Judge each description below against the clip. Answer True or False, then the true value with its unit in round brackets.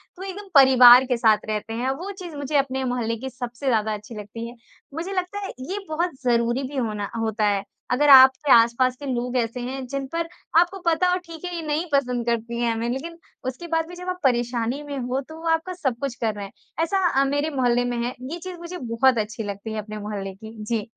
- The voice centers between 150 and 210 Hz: False (255 Hz)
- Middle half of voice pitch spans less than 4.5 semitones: False (5.5 semitones)